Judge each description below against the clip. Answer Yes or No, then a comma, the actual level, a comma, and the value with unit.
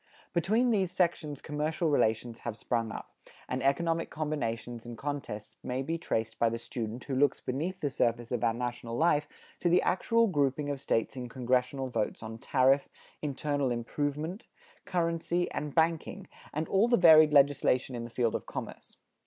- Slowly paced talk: No, average, 170 wpm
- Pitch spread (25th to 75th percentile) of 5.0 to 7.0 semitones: Yes, average, 5.3 semitones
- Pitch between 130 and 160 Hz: Yes, medium, 140 Hz